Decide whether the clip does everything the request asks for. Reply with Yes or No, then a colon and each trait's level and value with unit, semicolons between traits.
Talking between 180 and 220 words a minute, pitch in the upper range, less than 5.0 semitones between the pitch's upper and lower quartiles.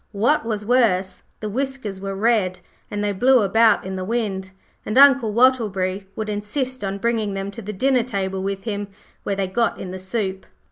Yes: average, 190 wpm; high, 205 Hz; average, 3.4 semitones